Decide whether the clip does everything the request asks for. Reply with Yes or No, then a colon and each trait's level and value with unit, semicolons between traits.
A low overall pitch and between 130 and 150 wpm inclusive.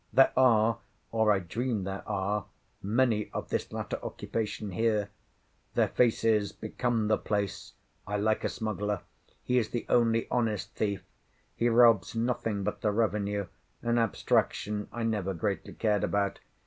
Yes: low, 110 Hz; average, 145 wpm